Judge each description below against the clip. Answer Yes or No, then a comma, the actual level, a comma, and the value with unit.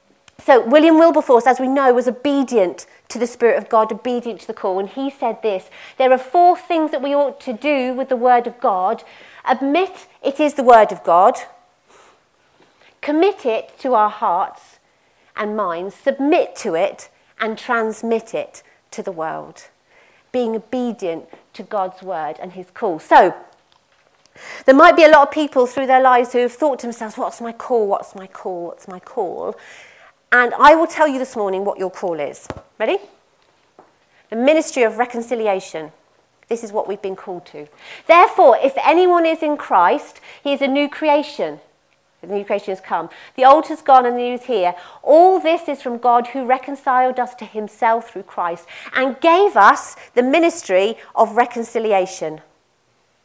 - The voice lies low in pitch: No, high, 245 Hz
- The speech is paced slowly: No, average, 180 wpm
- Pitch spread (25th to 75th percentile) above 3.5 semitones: Yes, average, 5.1 semitones